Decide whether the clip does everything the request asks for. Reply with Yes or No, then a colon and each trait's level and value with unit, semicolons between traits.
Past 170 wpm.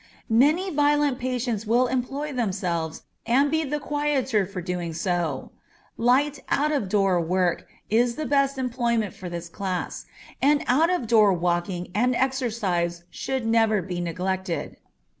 No: average, 140 wpm